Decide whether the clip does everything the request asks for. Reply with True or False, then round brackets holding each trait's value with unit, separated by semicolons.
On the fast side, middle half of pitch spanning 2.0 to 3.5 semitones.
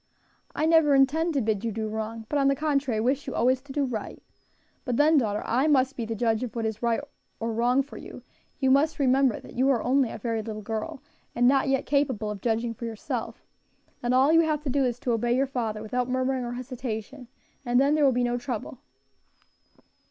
True (225 wpm; 3.2 semitones)